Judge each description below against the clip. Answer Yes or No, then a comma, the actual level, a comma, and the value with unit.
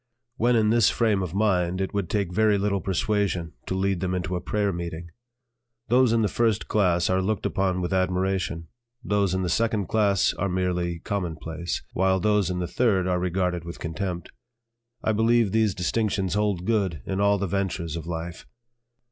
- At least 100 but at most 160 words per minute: No, average, 180 wpm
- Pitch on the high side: No, very low, 95 Hz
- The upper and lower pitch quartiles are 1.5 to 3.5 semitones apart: Yes, average, 2.8 semitones